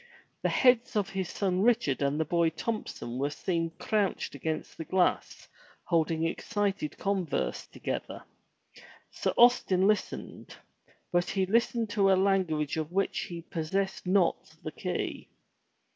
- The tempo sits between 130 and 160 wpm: Yes, slow, 135 wpm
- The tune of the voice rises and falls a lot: No, average, 3.8 semitones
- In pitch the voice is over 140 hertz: Yes, medium, 185 Hz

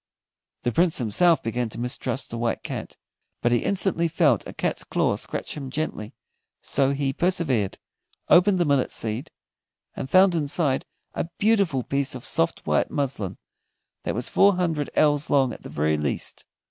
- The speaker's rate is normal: Yes, average, 165 wpm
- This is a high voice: No, medium, 140 Hz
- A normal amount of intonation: No, wide, 5.9 semitones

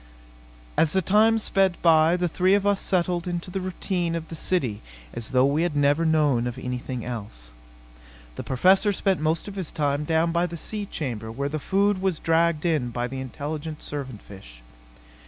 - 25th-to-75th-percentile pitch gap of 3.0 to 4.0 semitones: No, wide, 5.4 semitones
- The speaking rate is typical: Yes, average, 190 wpm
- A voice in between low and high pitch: Yes, medium, 160 Hz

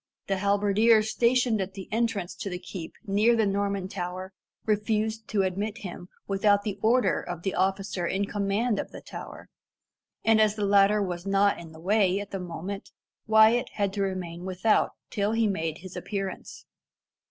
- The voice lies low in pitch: No, high, 200 Hz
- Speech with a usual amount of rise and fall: No, narrow, 2.3 semitones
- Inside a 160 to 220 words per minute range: Yes, average, 175 wpm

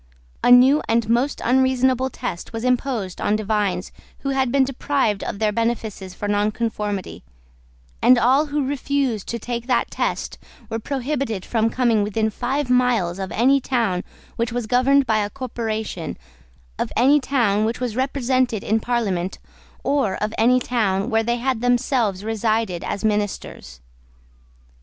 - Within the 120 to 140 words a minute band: No, average, 150 wpm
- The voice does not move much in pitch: No, average, 3.4 semitones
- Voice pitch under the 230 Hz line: No, high, 235 Hz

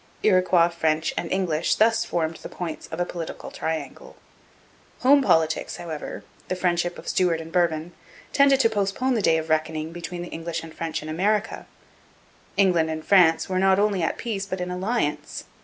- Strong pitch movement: No, average, 3.2 semitones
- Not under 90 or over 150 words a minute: No, average, 175 wpm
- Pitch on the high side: No, medium, 175 Hz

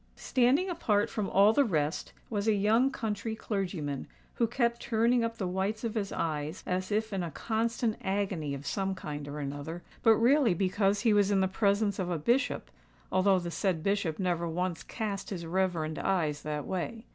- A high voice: Yes, high, 195 Hz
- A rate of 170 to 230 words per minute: Yes, average, 185 wpm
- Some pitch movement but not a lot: Yes, average, 4.4 semitones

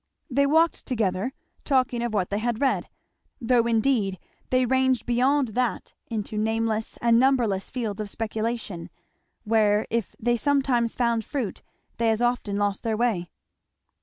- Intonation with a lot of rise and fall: No, average, 2.8 semitones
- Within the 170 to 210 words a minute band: No, average, 145 wpm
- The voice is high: Yes, high, 230 Hz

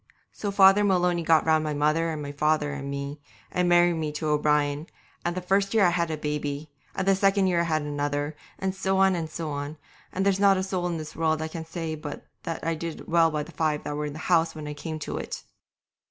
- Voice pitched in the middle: Yes, medium, 160 Hz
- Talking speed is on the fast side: Yes, fast, 240 wpm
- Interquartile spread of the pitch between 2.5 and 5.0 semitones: Yes, average, 3.0 semitones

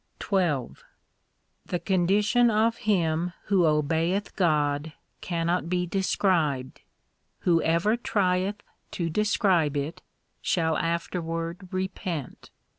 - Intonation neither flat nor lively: Yes, average, 3.0 semitones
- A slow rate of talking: Yes, slow, 90 wpm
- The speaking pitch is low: No, medium, 175 Hz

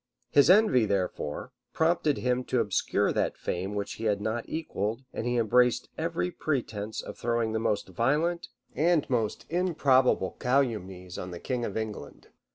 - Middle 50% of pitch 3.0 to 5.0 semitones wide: No, wide, 5.6 semitones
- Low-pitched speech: Yes, low, 120 Hz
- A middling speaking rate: Yes, average, 160 wpm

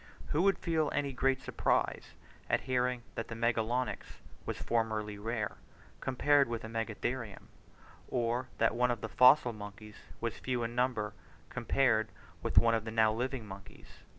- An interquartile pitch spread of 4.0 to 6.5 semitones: No, narrow, 2.5 semitones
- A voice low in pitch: Yes, low, 115 Hz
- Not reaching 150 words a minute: No, average, 155 wpm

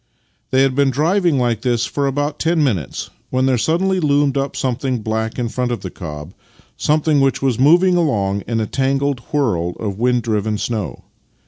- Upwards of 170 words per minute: Yes, average, 190 wpm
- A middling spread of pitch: Yes, average, 4.5 semitones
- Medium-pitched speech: No, low, 130 Hz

